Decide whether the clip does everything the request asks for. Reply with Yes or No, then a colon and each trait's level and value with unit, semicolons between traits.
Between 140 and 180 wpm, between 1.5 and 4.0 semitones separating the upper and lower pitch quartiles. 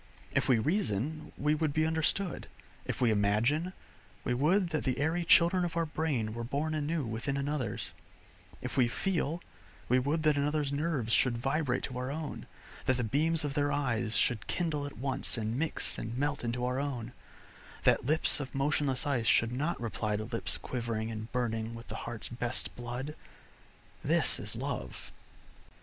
No: average, 175 wpm; average, 4.6 semitones